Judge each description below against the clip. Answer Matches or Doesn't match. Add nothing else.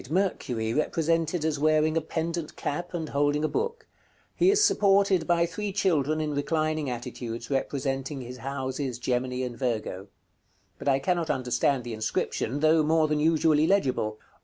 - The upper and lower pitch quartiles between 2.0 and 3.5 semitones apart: Doesn't match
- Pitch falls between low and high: Matches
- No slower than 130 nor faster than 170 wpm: Matches